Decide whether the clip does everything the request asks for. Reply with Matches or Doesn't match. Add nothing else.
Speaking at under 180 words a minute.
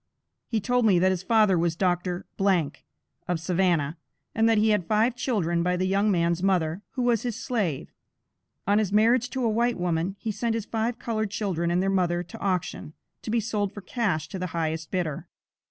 Doesn't match